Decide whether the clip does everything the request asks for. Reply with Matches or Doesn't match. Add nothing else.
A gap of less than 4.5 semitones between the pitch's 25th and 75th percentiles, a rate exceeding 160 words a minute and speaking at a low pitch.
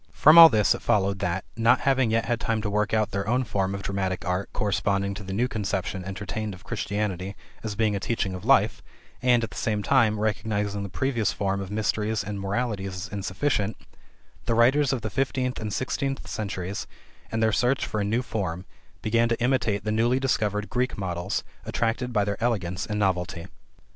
Matches